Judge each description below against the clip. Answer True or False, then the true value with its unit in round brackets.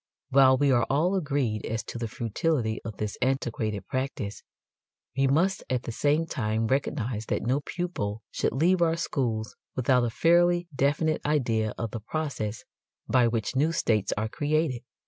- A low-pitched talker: True (130 Hz)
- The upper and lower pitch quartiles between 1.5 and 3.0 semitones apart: False (5.3 semitones)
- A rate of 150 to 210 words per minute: True (165 wpm)